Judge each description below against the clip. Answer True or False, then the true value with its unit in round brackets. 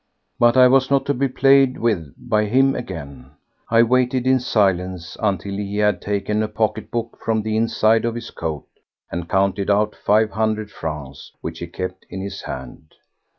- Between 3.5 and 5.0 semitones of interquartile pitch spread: True (4.2 semitones)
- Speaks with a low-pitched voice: True (105 Hz)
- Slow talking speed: False (180 wpm)